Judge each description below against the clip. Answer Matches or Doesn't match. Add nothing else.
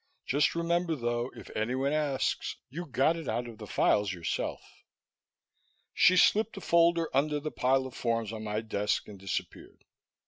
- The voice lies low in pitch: Matches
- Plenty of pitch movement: Matches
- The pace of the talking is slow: Doesn't match